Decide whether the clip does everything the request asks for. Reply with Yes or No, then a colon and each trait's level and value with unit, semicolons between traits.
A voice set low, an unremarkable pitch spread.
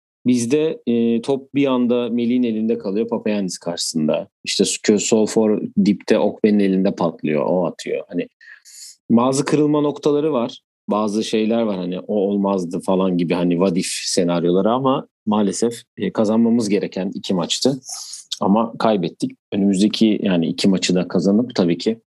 Yes: low, 110 Hz; average, 3.7 semitones